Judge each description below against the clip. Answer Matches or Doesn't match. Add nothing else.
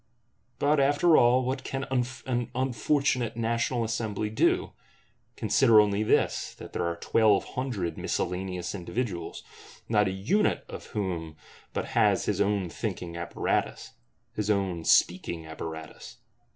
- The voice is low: Matches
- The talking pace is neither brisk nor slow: Doesn't match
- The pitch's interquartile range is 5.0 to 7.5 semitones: Matches